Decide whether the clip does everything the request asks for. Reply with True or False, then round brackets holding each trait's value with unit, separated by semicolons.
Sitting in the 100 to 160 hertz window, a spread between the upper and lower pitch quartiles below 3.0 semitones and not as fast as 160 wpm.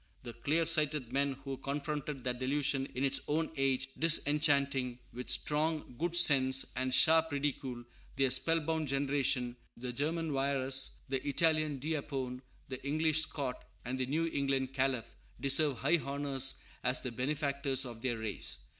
True (140 Hz; 2.5 semitones; 150 wpm)